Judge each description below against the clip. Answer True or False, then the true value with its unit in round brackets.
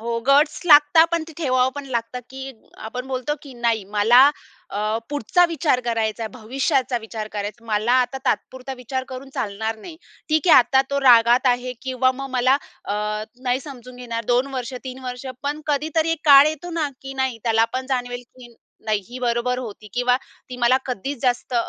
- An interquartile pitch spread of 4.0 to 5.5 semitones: False (2.5 semitones)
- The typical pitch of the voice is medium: False (255 Hz)